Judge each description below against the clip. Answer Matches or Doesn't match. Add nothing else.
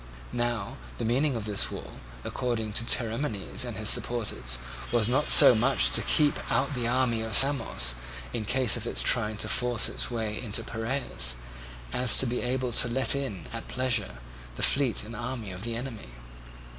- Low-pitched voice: Matches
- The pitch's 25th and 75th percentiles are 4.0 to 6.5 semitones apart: Doesn't match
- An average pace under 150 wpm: Doesn't match